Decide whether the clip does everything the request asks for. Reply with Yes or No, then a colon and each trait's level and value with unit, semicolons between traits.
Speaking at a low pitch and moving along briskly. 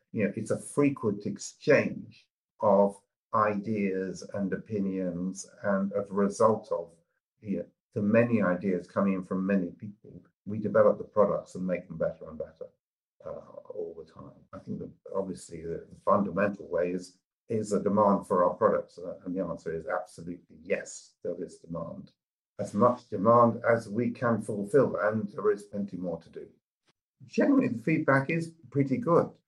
No: low, 115 Hz; average, 170 wpm